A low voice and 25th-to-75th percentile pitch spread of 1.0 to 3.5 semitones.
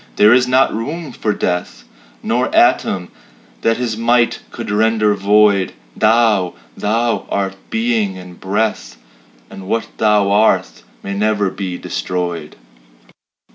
Yes: low, 105 Hz; average, 3.1 semitones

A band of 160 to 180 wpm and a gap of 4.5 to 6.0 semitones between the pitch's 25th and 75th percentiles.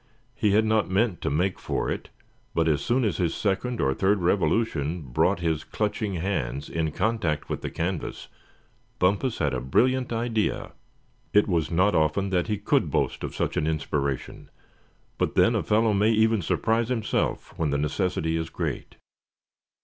Yes: average, 170 wpm; wide, 5.6 semitones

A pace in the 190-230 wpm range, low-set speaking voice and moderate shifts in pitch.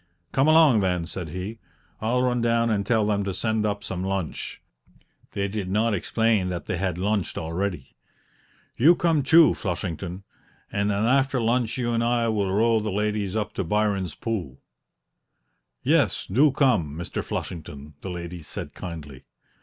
No: average, 160 wpm; low, 105 Hz; average, 4.1 semitones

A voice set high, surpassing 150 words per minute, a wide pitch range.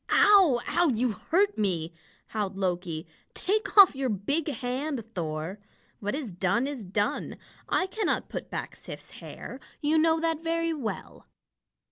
No: very high, 255 Hz; average, 145 wpm; wide, 8.6 semitones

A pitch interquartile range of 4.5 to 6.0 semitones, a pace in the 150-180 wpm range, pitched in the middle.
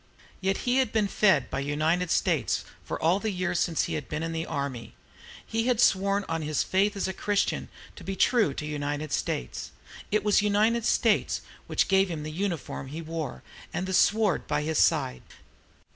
No: average, 5.0 semitones; average, 190 wpm; medium, 180 Hz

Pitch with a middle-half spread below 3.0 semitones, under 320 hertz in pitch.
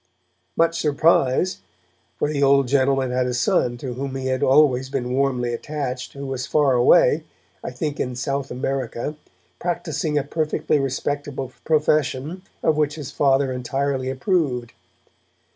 Yes: narrow, 2.5 semitones; low, 135 Hz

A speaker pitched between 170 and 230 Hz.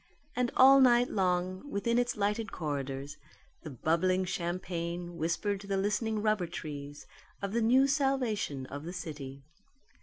Yes: medium, 185 Hz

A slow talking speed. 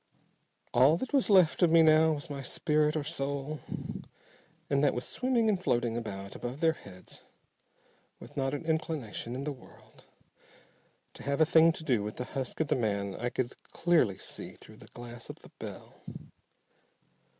No: average, 175 wpm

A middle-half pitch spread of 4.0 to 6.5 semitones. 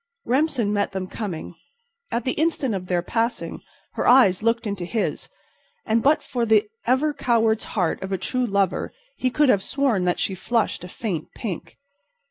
Yes: average, 4.6 semitones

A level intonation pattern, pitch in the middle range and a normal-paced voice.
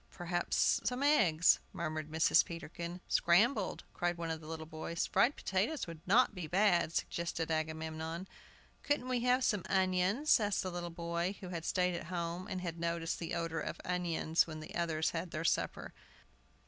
Yes: narrow, 2.3 semitones; medium, 170 Hz; average, 175 wpm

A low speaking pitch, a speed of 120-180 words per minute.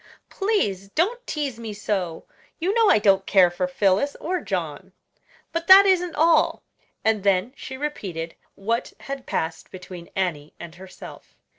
No: high, 210 Hz; average, 150 wpm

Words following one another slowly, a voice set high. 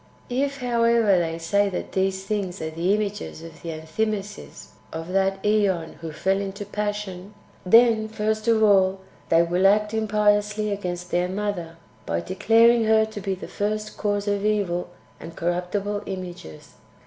No: average, 160 wpm; high, 200 Hz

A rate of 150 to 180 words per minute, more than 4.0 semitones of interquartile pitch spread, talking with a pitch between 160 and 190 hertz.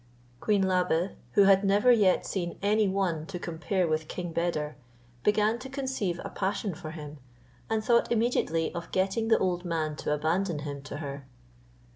Yes: average, 170 wpm; average, 4.4 semitones; medium, 185 Hz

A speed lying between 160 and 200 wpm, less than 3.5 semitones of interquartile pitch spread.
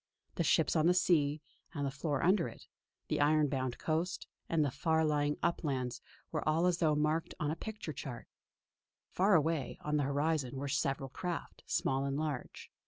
Yes: average, 180 wpm; average, 2.7 semitones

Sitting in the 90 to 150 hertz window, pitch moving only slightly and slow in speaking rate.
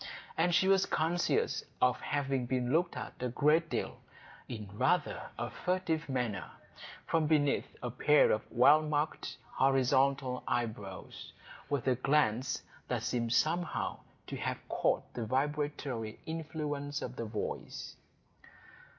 No: medium, 140 Hz; average, 4.1 semitones; slow, 130 wpm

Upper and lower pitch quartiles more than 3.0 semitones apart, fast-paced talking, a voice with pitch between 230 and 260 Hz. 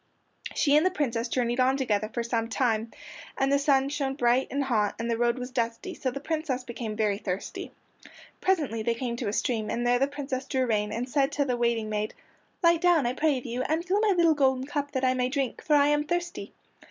Yes: average, 3.5 semitones; fast, 235 wpm; very high, 255 Hz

